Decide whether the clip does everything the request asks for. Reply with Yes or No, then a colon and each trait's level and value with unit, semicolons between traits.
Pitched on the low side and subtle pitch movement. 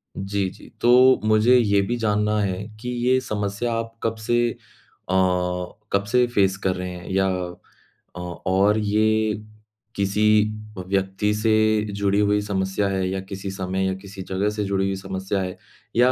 Yes: low, 100 Hz; narrow, 2.1 semitones